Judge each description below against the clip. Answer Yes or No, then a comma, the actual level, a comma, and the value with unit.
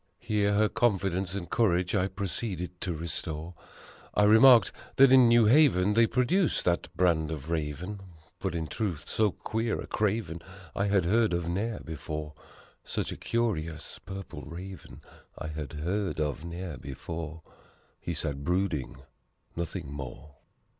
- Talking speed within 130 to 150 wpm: Yes, average, 145 wpm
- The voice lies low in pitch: Yes, very low, 90 Hz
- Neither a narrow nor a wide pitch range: Yes, average, 4.7 semitones